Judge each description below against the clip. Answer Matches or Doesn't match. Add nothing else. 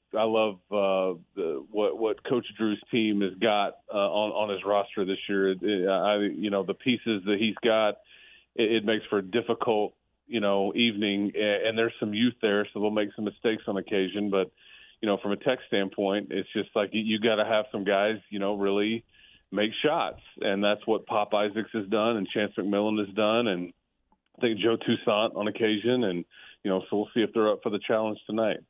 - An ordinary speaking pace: Doesn't match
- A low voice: Matches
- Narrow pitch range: Matches